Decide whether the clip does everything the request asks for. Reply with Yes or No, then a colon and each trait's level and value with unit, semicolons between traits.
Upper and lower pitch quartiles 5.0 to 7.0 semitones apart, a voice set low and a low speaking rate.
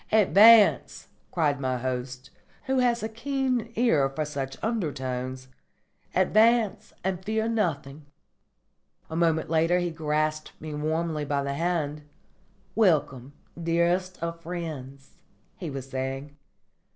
No: wide, 5.4 semitones; medium, 160 Hz; slow, 115 wpm